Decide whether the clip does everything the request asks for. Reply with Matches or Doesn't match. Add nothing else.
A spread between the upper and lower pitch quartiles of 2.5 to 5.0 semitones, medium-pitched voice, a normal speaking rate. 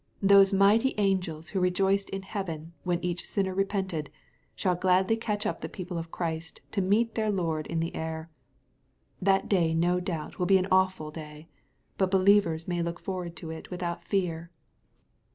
Matches